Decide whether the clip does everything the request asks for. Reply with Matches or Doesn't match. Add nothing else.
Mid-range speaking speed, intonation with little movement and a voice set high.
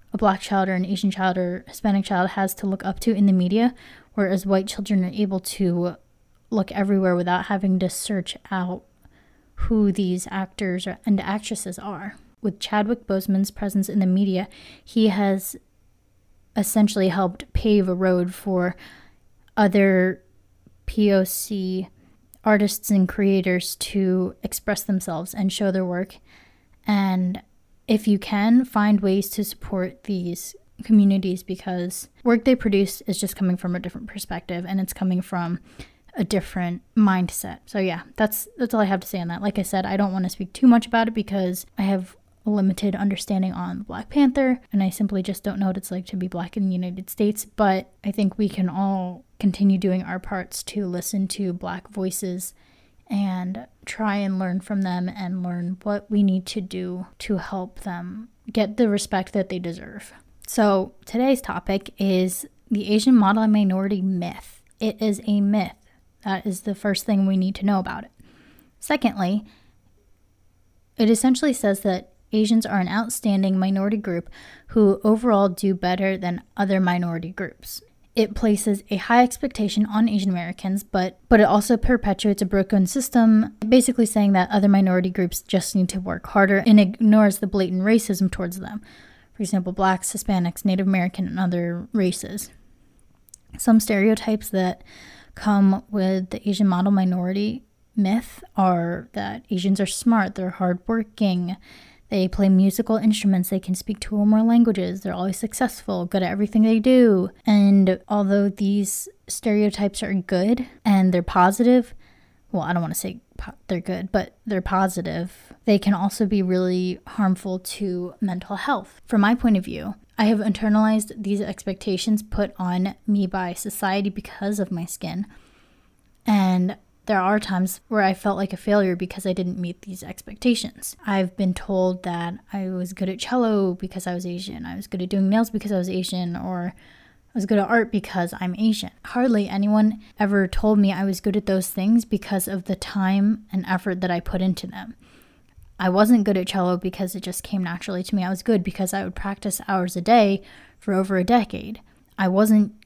Matches